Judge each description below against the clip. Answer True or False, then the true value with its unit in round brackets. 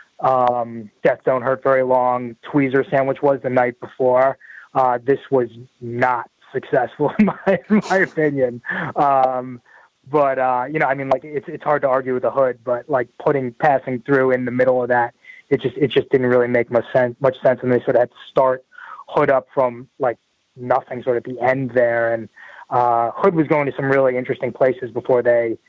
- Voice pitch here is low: True (130 Hz)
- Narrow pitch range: True (1.7 semitones)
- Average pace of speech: False (210 wpm)